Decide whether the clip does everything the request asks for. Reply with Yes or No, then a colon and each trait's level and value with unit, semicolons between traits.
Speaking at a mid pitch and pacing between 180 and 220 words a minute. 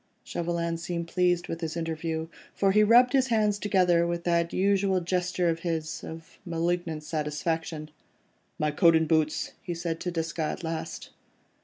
No: medium, 170 Hz; average, 160 wpm